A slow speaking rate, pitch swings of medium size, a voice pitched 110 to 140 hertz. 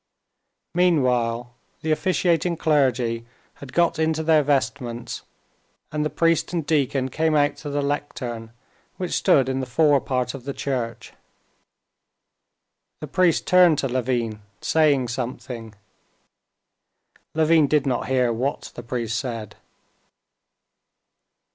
Yes: slow, 115 wpm; average, 4.2 semitones; low, 135 Hz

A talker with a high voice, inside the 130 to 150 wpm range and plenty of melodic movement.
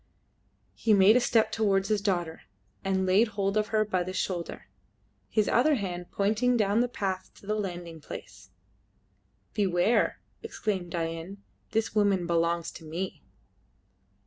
No: high, 195 Hz; average, 145 wpm; average, 3.3 semitones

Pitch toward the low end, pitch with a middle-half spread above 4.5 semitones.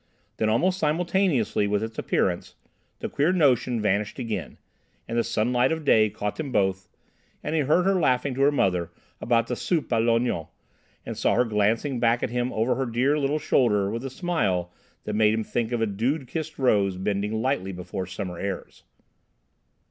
Yes: low, 115 Hz; average, 5.1 semitones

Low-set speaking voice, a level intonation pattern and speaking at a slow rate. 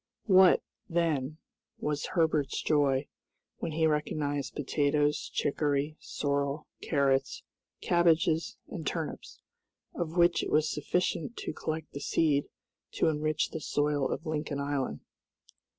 No: medium, 150 Hz; narrow, 2.1 semitones; slow, 120 wpm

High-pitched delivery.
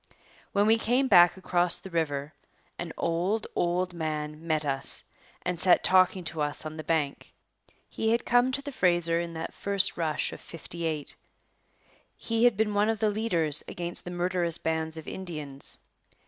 No: medium, 175 Hz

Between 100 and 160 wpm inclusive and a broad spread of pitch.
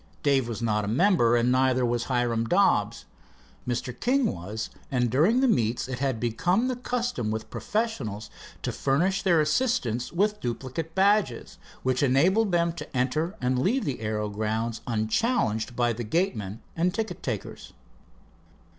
Yes: average, 155 wpm; wide, 8.2 semitones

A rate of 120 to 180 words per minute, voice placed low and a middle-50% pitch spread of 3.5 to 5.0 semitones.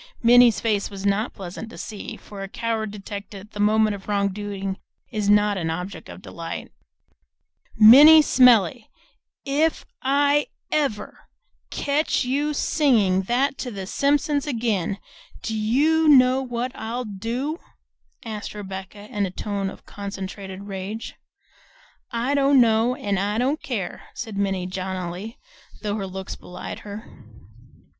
No: slow, 135 wpm; high, 215 Hz; average, 4.2 semitones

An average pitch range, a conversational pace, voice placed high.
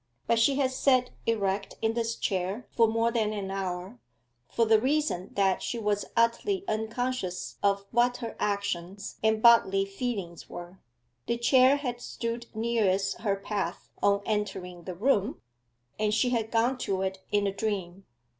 Yes: average, 3.3 semitones; average, 160 wpm; high, 215 Hz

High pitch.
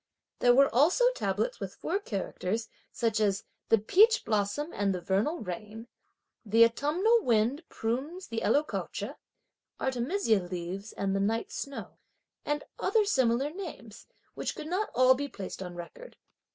Yes: high, 235 Hz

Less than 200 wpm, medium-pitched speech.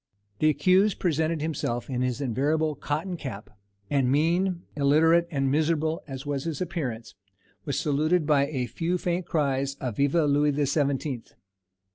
Yes: average, 150 wpm; medium, 150 Hz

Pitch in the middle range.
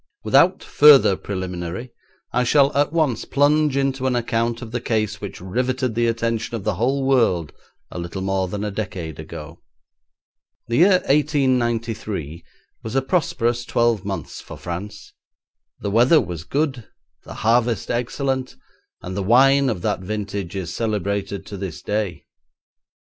No: low, 115 Hz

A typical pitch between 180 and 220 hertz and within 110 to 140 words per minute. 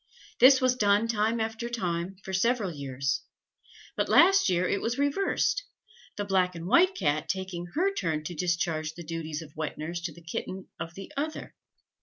No: high, 190 Hz; average, 180 wpm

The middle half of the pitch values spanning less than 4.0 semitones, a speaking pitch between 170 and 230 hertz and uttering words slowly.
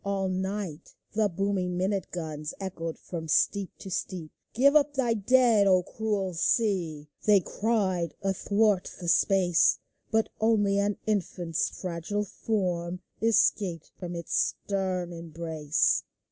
Yes: average, 3.3 semitones; high, 190 Hz; slow, 130 wpm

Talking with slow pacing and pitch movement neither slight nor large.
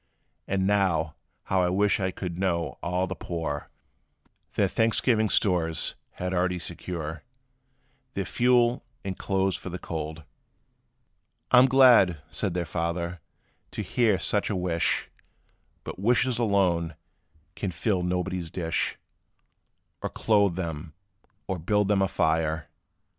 Yes: slow, 130 wpm; average, 3.2 semitones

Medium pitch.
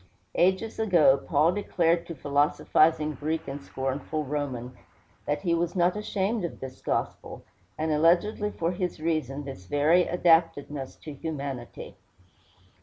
Yes: medium, 155 Hz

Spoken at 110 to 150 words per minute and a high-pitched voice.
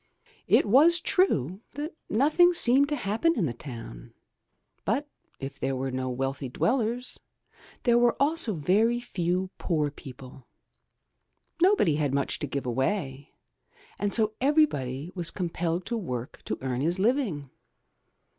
No: slow, 135 wpm; medium, 180 Hz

